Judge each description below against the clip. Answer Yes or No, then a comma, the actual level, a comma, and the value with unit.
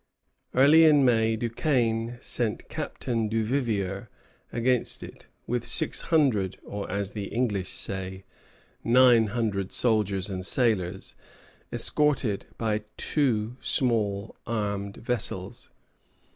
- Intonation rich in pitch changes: No, average, 3.5 semitones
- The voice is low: Yes, low, 115 Hz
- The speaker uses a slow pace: Yes, slow, 105 wpm